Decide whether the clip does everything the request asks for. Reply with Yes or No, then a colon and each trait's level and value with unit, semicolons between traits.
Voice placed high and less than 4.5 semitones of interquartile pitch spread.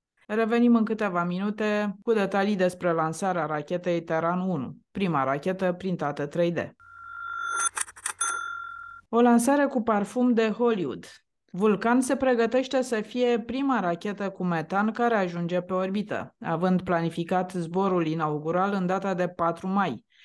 No: high, 200 Hz; average, 5.2 semitones